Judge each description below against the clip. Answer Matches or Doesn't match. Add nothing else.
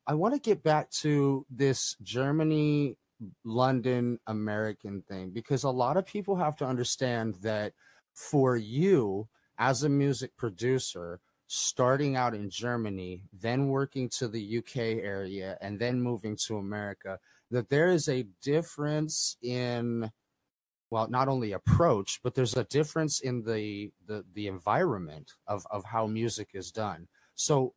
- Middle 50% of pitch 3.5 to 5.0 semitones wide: Matches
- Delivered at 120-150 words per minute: Matches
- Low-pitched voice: Matches